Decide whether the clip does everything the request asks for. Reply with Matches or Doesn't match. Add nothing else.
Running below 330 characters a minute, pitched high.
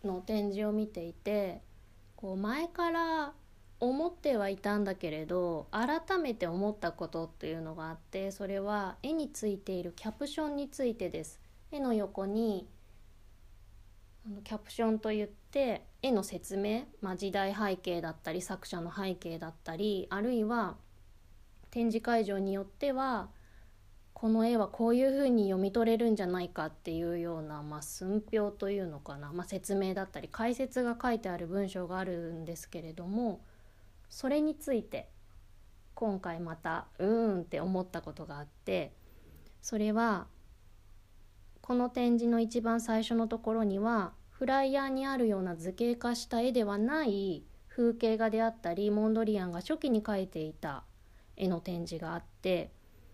Matches